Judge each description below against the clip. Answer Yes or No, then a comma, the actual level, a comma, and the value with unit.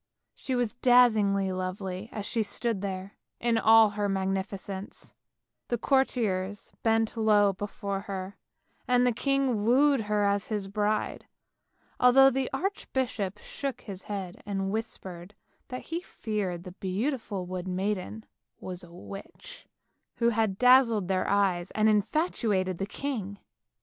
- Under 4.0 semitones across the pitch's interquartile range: Yes, average, 3.6 semitones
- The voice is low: No, high, 205 Hz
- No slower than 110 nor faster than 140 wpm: Yes, slow, 135 wpm